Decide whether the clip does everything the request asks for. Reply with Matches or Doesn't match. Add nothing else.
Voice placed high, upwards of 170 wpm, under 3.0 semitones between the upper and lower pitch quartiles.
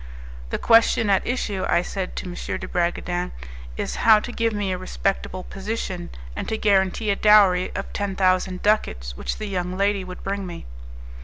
Matches